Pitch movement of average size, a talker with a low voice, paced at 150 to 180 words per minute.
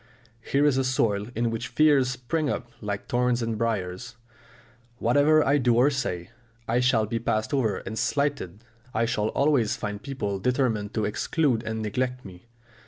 Yes: average, 3.6 semitones; low, 120 Hz; average, 170 wpm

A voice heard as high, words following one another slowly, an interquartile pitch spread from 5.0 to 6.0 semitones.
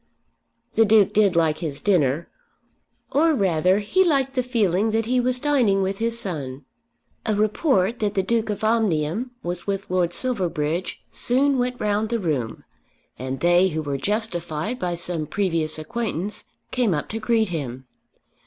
No: high, 200 Hz; average, 160 wpm; wide, 5.6 semitones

